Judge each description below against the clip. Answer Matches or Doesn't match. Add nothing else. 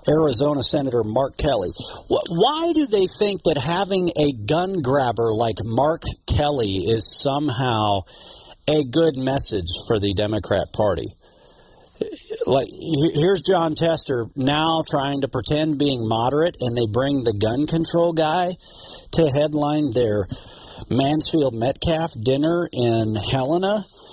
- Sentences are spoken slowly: Matches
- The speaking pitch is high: Doesn't match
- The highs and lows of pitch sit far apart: Matches